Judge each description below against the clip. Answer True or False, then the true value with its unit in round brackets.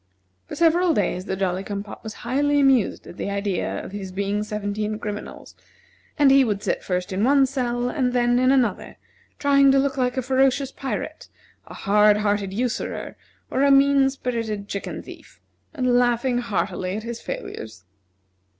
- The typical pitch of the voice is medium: False (240 Hz)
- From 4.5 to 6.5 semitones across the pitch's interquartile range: True (4.8 semitones)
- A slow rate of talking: False (170 wpm)